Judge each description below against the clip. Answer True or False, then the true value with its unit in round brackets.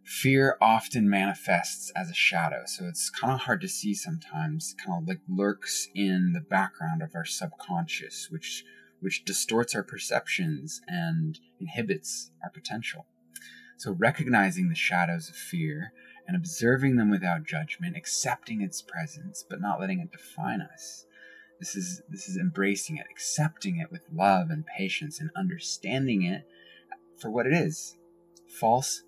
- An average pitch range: False (6.9 semitones)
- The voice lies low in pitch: False (165 Hz)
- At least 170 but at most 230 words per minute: False (150 wpm)